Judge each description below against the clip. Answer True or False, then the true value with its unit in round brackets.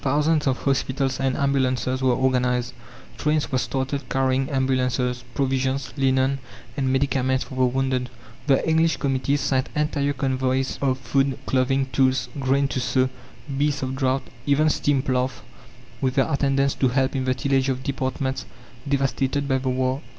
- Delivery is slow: False (155 wpm)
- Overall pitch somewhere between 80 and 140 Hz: True (135 Hz)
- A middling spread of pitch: False (1.2 semitones)